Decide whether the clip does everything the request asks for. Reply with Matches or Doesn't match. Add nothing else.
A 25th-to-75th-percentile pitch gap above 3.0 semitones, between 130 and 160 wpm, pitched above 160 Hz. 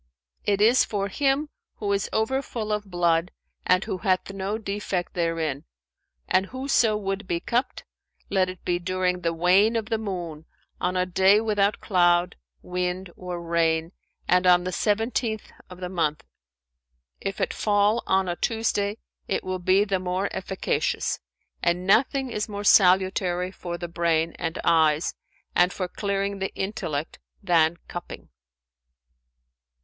Doesn't match